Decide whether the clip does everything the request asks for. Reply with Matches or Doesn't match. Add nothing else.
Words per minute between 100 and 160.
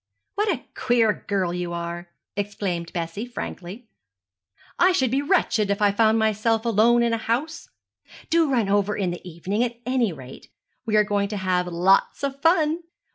Doesn't match